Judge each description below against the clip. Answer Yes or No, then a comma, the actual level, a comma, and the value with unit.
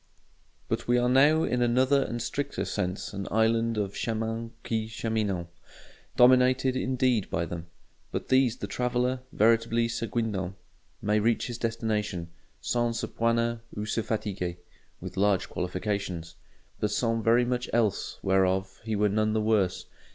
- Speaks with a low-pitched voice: Yes, low, 115 Hz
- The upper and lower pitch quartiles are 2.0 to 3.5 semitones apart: Yes, average, 2.8 semitones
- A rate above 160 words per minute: No, average, 150 wpm